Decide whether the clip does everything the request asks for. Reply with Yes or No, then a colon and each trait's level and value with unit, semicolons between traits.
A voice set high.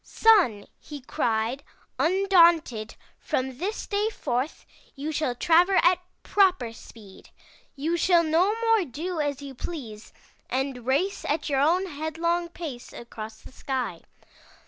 Yes: very high, 305 Hz